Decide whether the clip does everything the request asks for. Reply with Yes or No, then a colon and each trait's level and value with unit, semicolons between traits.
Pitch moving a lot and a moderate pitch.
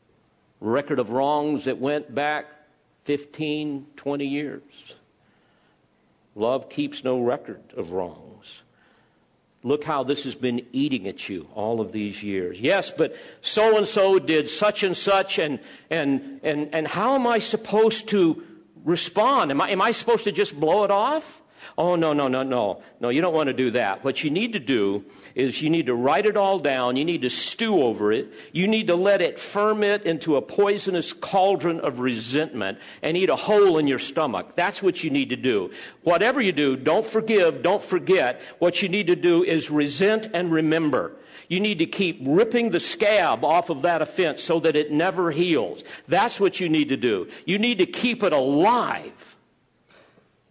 Yes: wide, 6.5 semitones; medium, 160 Hz